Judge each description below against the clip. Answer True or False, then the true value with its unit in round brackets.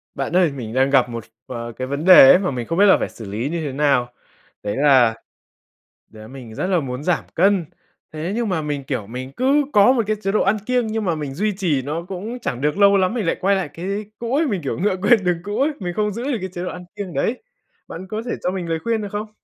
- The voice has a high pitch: False (180 Hz)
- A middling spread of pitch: False (7.1 semitones)